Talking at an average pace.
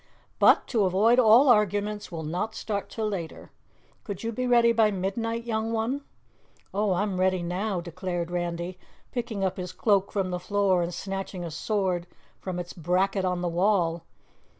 Yes: average, 170 wpm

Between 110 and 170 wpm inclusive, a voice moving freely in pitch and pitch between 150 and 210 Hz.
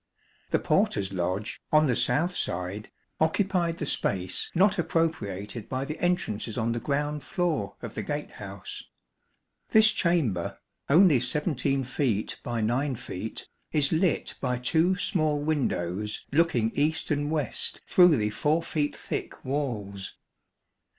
No: slow, 135 wpm; wide, 6.9 semitones; medium, 140 Hz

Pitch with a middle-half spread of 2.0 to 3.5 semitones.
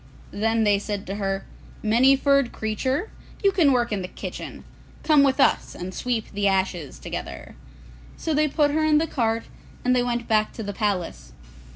No: average, 5.3 semitones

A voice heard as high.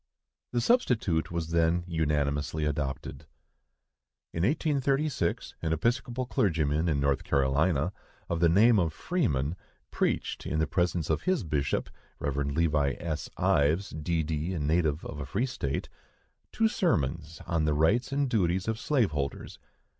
No: very low, 80 Hz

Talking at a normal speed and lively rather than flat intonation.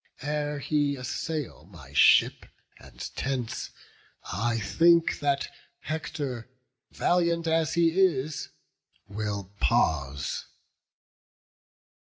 No: slow, 85 wpm; wide, 6.9 semitones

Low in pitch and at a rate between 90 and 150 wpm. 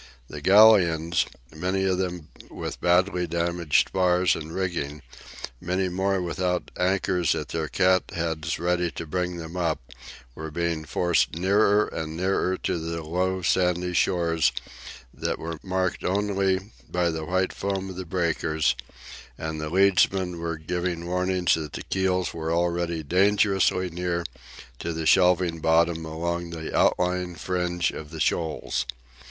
Yes: very low, 90 Hz; average, 140 wpm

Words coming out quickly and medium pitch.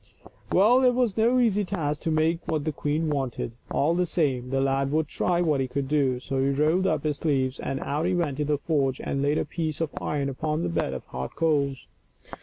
Yes: fast, 230 wpm; medium, 150 Hz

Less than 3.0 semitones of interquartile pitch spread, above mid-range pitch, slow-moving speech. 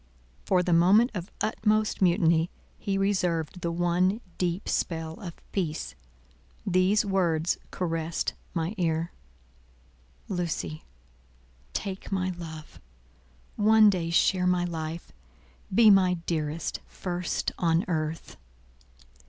No: narrow, 2.6 semitones; medium, 175 Hz; slow, 105 wpm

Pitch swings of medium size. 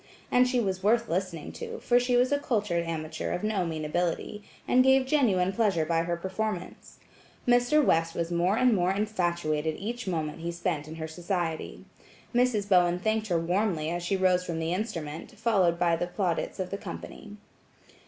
Yes: average, 4.4 semitones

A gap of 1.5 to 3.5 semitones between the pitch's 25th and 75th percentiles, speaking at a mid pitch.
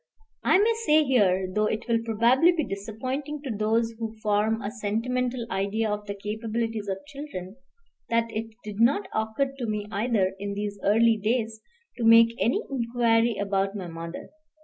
No: narrow, 2.6 semitones; high, 225 Hz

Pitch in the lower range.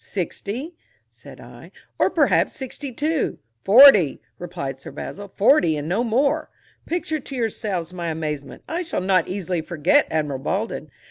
No: high, 195 Hz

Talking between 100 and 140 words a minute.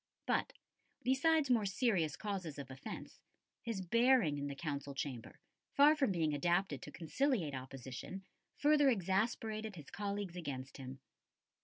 Yes: slow, 135 wpm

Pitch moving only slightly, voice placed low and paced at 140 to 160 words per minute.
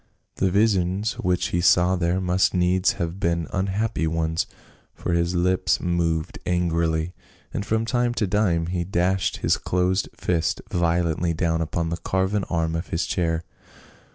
Yes: narrow, 2.0 semitones; very low, 90 Hz; average, 155 wpm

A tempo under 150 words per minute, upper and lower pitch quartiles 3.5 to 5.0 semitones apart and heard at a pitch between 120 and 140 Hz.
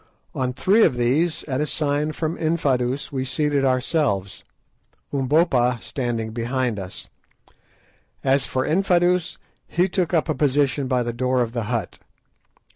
Yes: average, 140 wpm; average, 4.0 semitones; low, 135 Hz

